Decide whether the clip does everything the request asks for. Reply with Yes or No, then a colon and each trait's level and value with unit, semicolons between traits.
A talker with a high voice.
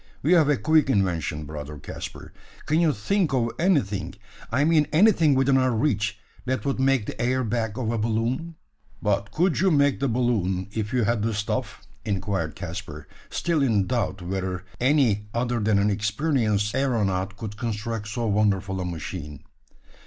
No: low, 115 Hz